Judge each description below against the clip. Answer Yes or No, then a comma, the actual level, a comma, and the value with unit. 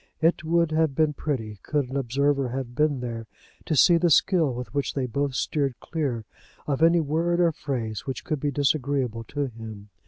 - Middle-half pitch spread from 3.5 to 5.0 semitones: Yes, average, 3.9 semitones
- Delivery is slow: No, average, 190 wpm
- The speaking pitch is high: No, medium, 140 Hz